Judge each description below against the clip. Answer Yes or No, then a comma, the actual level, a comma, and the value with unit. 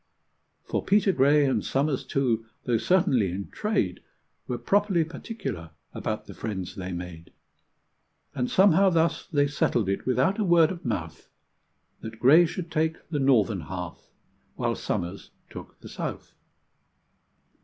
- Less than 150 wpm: Yes, average, 140 wpm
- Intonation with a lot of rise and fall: Yes, wide, 8.9 semitones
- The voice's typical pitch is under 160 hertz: Yes, low, 135 Hz